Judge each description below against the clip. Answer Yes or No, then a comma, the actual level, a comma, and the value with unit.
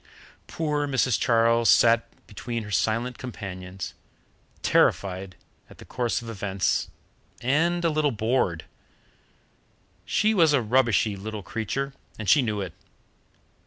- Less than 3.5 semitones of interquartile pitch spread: No, average, 4.4 semitones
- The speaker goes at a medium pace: No, slow, 125 wpm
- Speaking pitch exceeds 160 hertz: No, low, 115 Hz